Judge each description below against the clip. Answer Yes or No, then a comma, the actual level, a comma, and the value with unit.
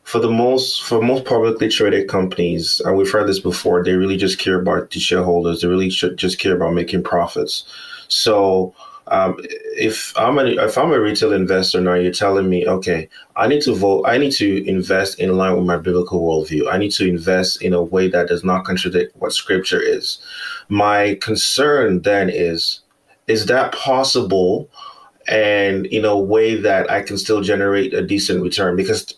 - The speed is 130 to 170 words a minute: No, average, 190 wpm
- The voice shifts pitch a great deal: No, average, 3.5 semitones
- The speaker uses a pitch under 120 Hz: Yes, very low, 95 Hz